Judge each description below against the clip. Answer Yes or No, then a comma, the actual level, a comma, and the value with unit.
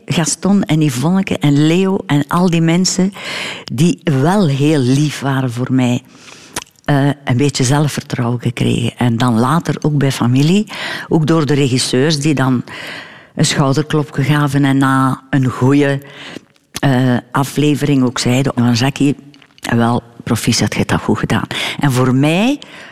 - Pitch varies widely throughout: No, average, 3.0 semitones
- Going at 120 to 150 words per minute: Yes, average, 140 wpm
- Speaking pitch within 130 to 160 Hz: Yes, medium, 140 Hz